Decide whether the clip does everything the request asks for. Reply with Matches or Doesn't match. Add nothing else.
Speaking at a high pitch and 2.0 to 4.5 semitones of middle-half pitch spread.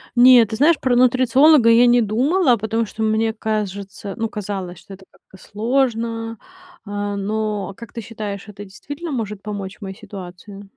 Matches